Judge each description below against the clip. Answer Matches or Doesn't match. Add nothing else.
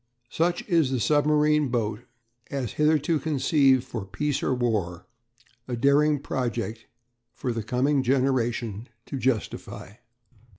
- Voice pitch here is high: Doesn't match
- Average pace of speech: Doesn't match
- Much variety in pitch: Doesn't match